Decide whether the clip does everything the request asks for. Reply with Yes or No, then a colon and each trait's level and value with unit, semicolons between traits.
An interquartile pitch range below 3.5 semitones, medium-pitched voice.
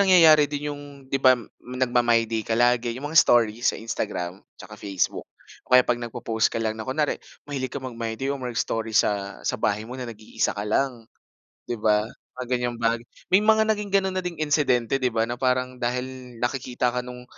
No: average, 3.0 semitones; low, 125 Hz